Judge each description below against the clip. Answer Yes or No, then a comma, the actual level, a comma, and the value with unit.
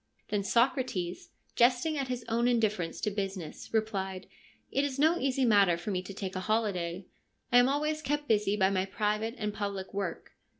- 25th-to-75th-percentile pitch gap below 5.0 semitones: Yes, average, 4.5 semitones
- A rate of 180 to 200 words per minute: Yes, average, 185 wpm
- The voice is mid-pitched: No, high, 210 Hz